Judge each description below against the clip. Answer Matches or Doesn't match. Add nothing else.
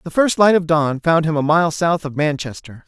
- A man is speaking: Matches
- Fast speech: Matches